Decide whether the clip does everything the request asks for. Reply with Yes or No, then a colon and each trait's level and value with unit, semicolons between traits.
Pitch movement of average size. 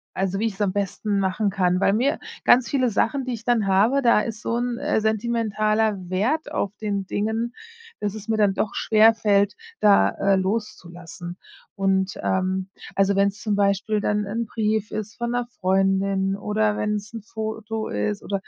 No: narrow, 2.2 semitones